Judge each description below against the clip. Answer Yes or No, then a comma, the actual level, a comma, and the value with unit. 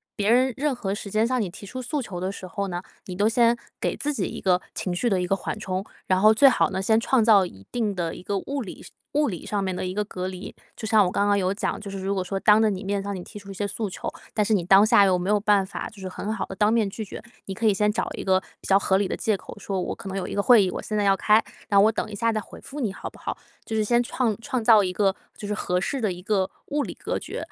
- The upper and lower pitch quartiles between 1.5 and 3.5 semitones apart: Yes, narrow, 2.5 semitones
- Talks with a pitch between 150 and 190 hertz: No, high, 205 Hz